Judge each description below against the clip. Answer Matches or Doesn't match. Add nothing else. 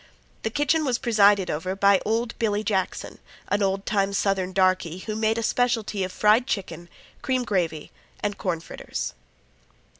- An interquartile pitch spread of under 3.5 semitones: Matches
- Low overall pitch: Doesn't match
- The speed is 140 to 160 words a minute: Matches